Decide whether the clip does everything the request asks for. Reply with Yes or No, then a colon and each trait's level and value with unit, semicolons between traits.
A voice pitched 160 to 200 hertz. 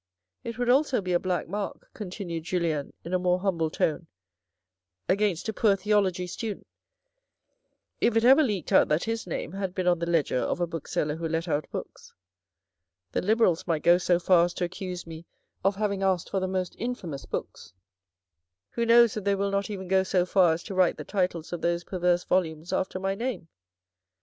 Yes: medium, 185 Hz